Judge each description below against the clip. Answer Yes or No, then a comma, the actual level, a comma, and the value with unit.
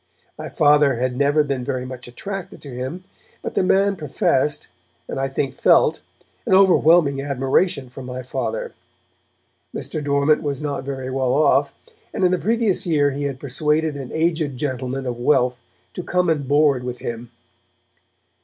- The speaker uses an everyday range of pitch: Yes, average, 3.5 semitones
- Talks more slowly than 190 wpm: Yes, average, 165 wpm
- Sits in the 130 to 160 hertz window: Yes, medium, 140 Hz